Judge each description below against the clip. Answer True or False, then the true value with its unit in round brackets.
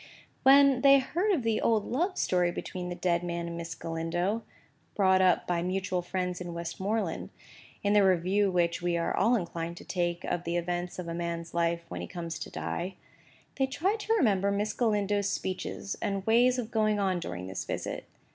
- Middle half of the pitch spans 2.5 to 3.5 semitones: False (3.9 semitones)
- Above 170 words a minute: True (185 wpm)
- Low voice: False (185 Hz)